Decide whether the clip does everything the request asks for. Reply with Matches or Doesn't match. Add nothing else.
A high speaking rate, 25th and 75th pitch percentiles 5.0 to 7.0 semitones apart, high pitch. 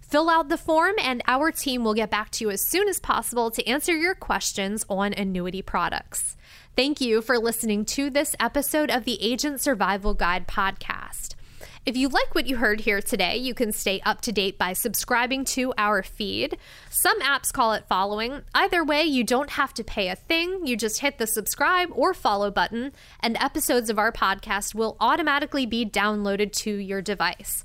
Doesn't match